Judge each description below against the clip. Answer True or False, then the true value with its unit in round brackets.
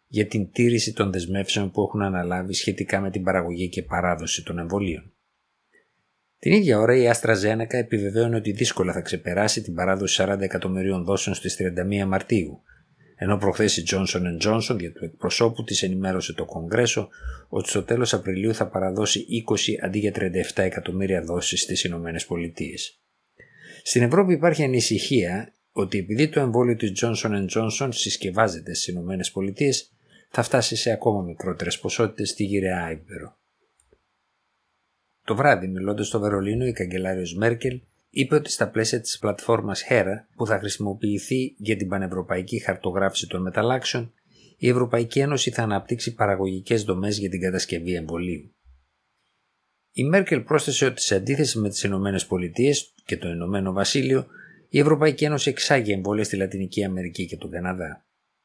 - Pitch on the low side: True (100 Hz)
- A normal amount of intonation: True (3.9 semitones)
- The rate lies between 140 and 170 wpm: True (150 wpm)